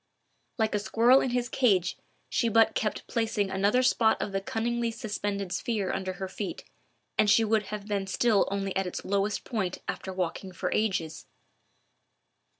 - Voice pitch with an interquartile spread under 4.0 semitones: Yes, average, 2.7 semitones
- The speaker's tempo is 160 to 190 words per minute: Yes, average, 165 wpm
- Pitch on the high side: Yes, high, 205 Hz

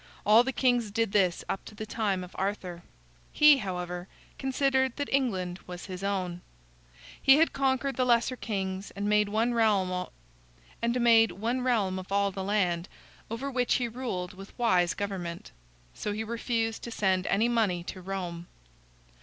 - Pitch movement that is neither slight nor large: Yes, average, 4.4 semitones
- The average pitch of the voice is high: Yes, high, 205 Hz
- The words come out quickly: No, average, 155 wpm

